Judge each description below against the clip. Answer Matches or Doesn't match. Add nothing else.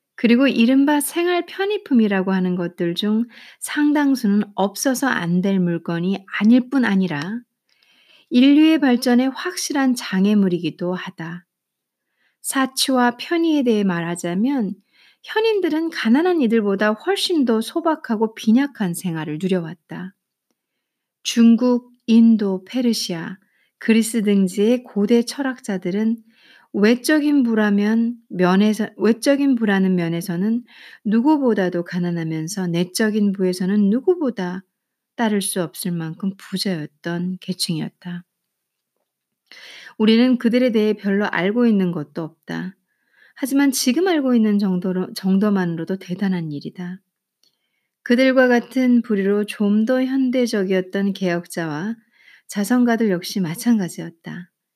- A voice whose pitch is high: Matches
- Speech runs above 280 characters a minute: Doesn't match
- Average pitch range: Matches